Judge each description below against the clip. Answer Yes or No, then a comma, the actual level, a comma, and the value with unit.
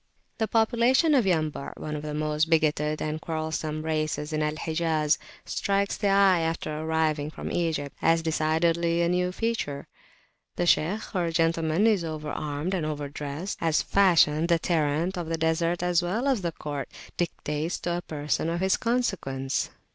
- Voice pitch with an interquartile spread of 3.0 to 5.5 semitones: No, narrow, 2.6 semitones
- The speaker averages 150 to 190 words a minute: Yes, average, 170 wpm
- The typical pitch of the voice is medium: Yes, medium, 165 Hz